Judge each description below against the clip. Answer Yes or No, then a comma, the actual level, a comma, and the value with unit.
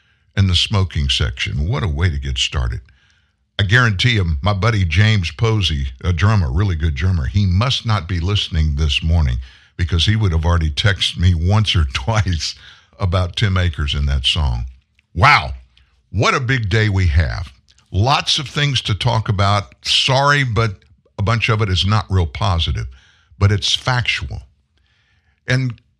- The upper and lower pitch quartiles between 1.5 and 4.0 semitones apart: No, average, 5.0 semitones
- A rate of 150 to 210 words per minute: Yes, average, 165 wpm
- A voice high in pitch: No, very low, 95 Hz